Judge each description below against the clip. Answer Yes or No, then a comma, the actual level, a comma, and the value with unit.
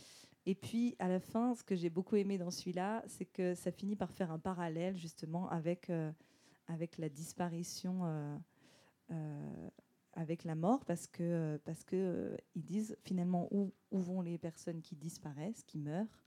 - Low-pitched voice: No, medium, 175 Hz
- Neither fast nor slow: Yes, average, 175 wpm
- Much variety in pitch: No, narrow, 2.5 semitones